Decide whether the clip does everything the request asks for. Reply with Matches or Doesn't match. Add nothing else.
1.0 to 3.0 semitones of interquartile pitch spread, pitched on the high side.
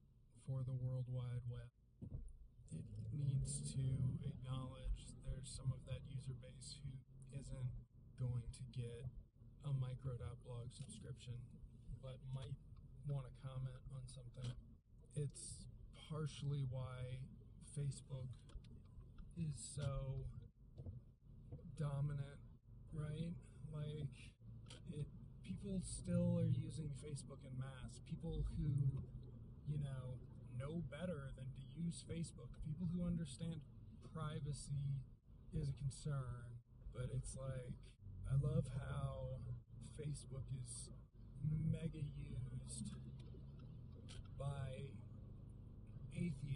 Doesn't match